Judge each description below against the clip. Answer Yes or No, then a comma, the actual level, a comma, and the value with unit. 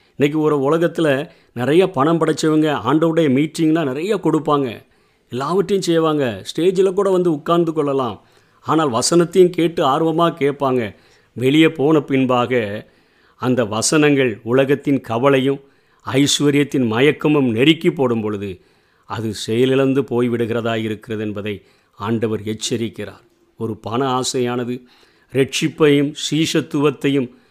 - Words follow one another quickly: No, average, 100 wpm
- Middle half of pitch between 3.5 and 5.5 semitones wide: Yes, average, 4.6 semitones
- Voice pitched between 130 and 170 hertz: Yes, medium, 140 Hz